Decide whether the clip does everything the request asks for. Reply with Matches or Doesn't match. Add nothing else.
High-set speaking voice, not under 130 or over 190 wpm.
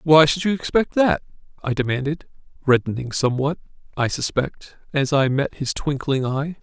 Doesn't match